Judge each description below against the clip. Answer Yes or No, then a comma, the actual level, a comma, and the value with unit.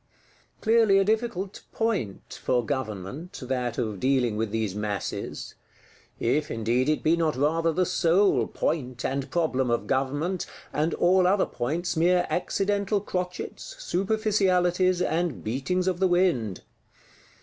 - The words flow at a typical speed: No, slow, 125 wpm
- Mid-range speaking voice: Yes, medium, 165 Hz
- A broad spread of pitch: Yes, wide, 6.5 semitones